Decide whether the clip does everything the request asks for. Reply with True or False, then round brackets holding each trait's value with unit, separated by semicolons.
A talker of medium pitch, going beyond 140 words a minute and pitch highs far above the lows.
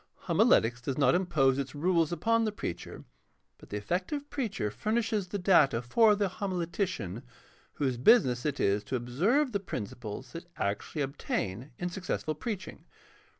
True (165 Hz; 150 wpm; 8.5 semitones)